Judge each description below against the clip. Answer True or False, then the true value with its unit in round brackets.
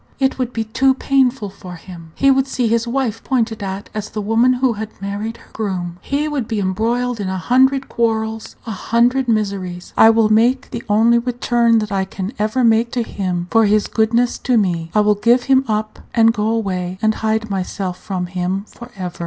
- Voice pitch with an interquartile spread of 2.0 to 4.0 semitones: True (3.4 semitones)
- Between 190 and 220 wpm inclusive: True (205 wpm)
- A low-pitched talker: False (220 Hz)